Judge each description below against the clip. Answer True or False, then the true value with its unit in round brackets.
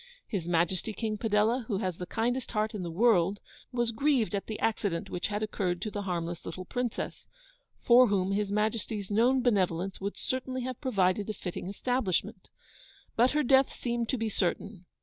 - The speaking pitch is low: False (210 Hz)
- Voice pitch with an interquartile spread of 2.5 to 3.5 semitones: False (4.2 semitones)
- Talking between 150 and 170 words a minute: False (180 wpm)